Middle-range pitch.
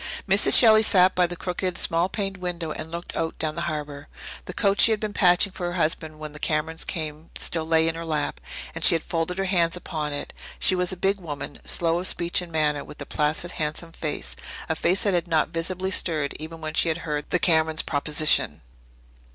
Yes: medium, 165 Hz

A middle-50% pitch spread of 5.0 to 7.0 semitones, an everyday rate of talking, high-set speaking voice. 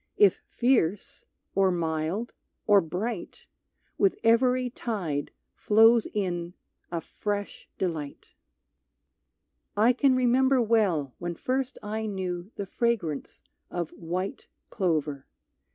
No: wide, 5.5 semitones; slow, 105 wpm; high, 200 Hz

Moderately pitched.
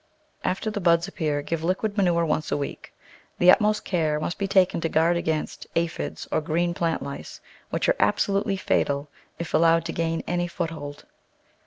Yes: medium, 170 Hz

